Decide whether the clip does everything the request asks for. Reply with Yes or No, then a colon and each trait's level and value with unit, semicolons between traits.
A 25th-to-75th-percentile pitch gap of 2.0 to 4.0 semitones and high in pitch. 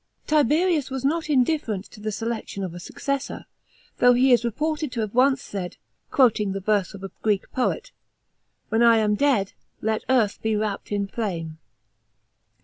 No: average, 4.8 semitones; high, 225 Hz